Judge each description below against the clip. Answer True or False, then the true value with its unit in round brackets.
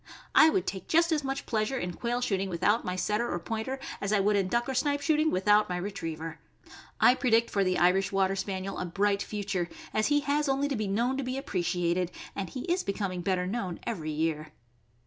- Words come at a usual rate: False (215 wpm)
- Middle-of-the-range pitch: False (205 Hz)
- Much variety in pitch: True (5.7 semitones)